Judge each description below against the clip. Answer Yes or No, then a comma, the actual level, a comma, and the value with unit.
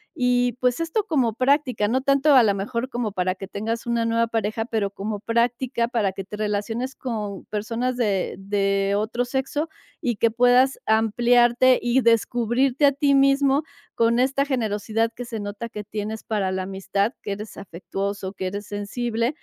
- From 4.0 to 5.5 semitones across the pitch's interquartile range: No, average, 3.4 semitones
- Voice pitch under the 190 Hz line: No, high, 230 Hz